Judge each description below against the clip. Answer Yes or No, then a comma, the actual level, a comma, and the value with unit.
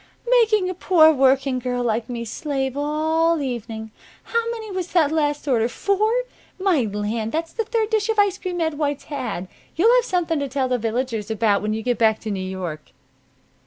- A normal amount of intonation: No, wide, 7.9 semitones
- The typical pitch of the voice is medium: No, very high, 285 Hz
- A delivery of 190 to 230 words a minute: Yes, average, 195 wpm